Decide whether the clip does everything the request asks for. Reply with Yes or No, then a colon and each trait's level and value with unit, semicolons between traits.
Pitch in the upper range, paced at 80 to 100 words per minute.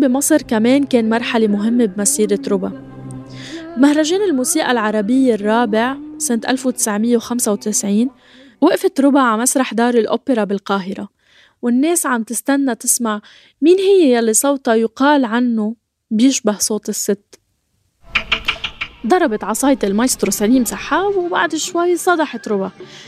No: high, 240 Hz; average, 110 wpm